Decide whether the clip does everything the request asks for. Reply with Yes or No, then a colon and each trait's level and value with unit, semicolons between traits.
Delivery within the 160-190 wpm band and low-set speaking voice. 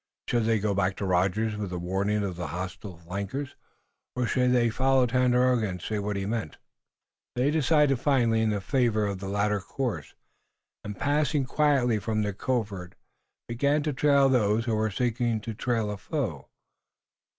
Yes: average, 170 wpm; low, 110 Hz